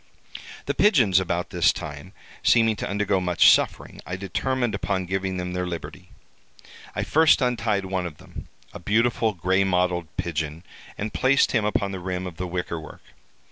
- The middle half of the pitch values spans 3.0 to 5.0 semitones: Yes, average, 3.3 semitones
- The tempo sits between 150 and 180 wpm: Yes, average, 170 wpm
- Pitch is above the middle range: No, very low, 95 Hz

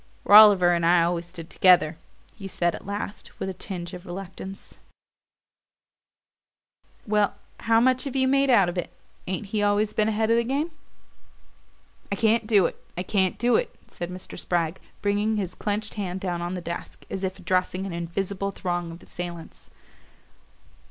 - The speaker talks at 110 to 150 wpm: No, average, 170 wpm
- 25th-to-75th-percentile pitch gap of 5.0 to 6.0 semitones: No, average, 3.3 semitones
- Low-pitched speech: No, high, 195 Hz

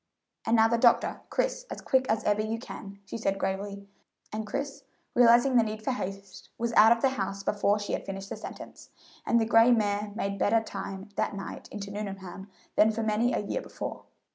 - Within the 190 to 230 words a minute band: Yes, fast, 205 wpm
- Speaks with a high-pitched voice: Yes, high, 215 Hz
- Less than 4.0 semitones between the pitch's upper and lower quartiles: Yes, average, 2.7 semitones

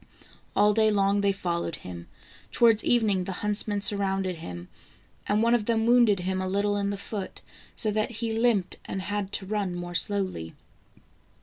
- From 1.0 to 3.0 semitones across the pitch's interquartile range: Yes, narrow, 2.4 semitones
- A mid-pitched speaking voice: No, high, 200 Hz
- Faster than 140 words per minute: Yes, average, 180 wpm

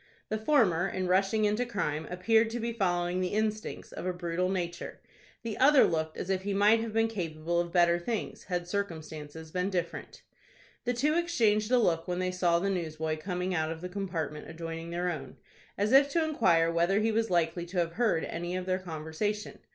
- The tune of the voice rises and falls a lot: No, average, 4.1 semitones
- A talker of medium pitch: Yes, medium, 180 Hz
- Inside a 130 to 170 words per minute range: No, average, 200 wpm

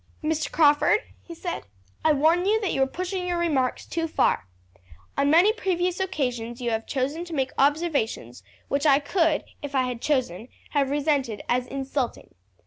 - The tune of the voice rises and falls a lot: No, average, 4.6 semitones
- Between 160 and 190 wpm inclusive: Yes, average, 170 wpm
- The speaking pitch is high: Yes, very high, 290 Hz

